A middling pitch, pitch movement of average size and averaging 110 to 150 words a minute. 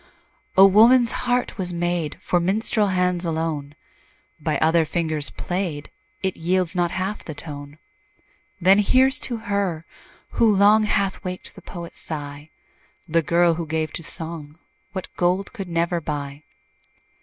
Yes: medium, 175 Hz; average, 3.5 semitones; average, 145 wpm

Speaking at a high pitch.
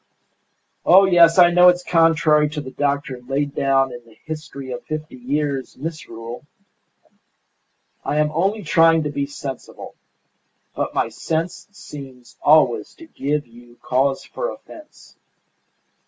No: medium, 150 Hz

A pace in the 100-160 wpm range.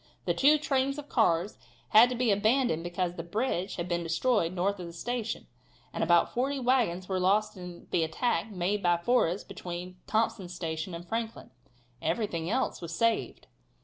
No: average, 175 wpm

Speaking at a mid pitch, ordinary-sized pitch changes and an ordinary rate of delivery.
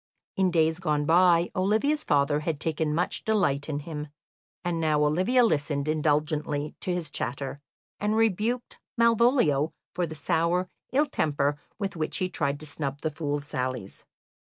Yes: medium, 160 Hz; average, 4.0 semitones; average, 155 wpm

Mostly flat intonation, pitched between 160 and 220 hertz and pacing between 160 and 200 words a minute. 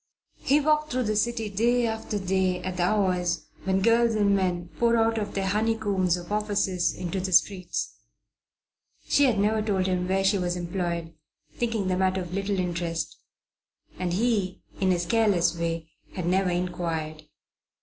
No: average, 3.2 semitones; high, 190 Hz; average, 165 wpm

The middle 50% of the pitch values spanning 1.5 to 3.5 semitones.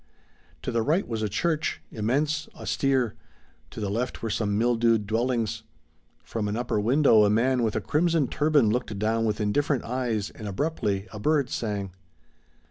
No: average, 4.3 semitones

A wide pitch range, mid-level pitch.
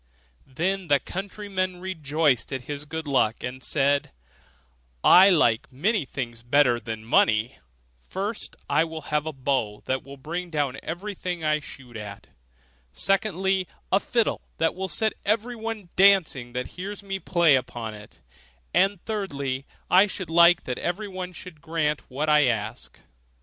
Yes: wide, 6.3 semitones; medium, 160 Hz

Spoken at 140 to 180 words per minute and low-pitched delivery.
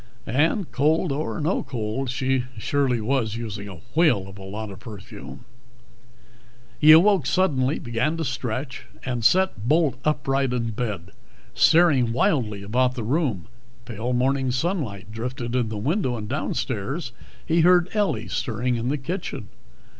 Yes: average, 145 wpm; low, 125 Hz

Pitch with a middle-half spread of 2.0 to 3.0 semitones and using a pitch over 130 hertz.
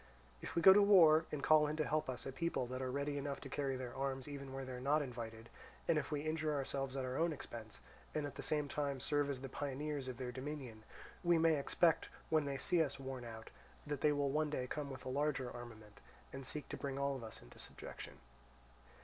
Yes: average, 2.7 semitones; medium, 140 Hz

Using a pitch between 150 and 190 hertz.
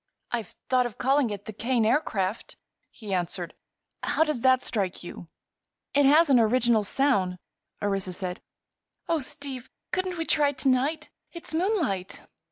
No: very high, 250 Hz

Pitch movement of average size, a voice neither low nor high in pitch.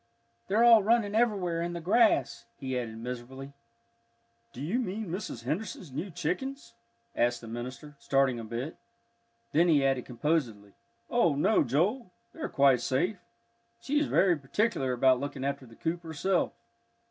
No: wide, 7.5 semitones; medium, 150 Hz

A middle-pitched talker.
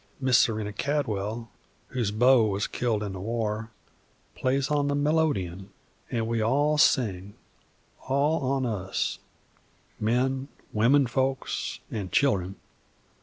No: low, 120 Hz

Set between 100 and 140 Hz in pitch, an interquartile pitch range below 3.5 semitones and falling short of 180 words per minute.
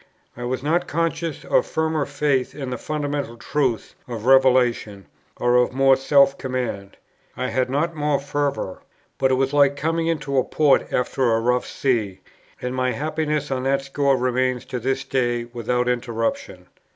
Yes: low, 135 Hz; average, 2.8 semitones; average, 165 wpm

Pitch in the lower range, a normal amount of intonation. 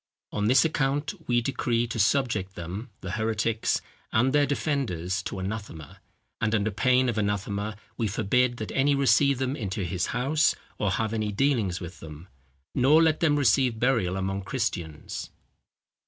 Yes: low, 115 Hz; average, 5.0 semitones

